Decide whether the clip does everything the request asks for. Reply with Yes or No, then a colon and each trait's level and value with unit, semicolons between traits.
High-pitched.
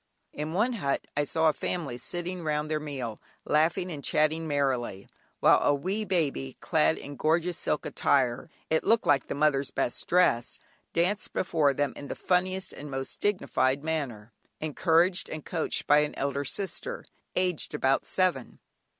No: medium, 155 Hz